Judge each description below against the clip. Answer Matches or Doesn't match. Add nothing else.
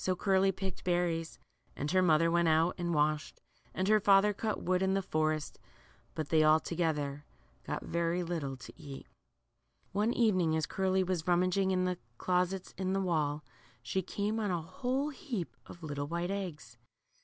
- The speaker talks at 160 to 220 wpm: Matches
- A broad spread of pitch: Doesn't match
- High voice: Doesn't match